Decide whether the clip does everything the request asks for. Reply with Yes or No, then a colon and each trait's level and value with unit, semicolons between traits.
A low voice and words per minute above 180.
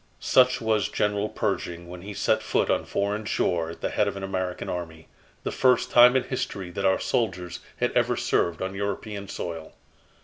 Yes: low, 100 Hz; average, 190 wpm